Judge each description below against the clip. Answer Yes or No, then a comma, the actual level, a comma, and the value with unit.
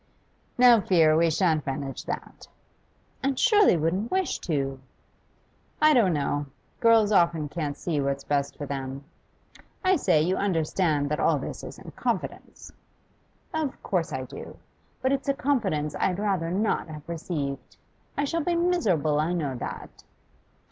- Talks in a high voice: No, medium, 170 Hz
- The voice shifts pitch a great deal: Yes, wide, 7.7 semitones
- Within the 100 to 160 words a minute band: Yes, average, 155 wpm